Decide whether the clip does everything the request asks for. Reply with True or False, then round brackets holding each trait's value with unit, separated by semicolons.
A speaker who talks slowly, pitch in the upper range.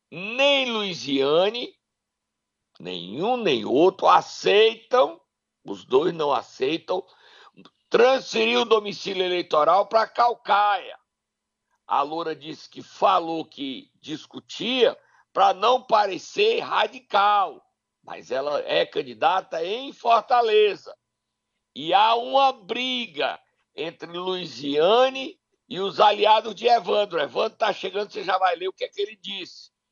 True (115 wpm; 230 Hz)